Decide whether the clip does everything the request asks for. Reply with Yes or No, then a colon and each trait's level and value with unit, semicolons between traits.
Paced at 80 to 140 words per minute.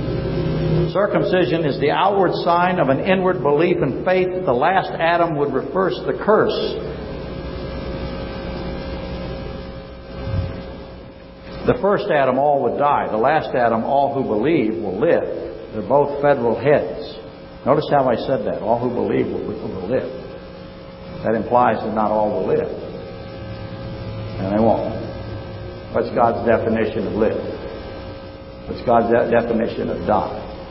Yes: slow, 135 wpm